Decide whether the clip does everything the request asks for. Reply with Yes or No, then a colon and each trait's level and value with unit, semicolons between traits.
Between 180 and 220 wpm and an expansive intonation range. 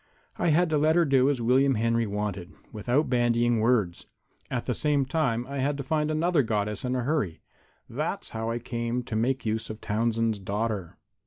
No: average, 190 wpm; average, 4.0 semitones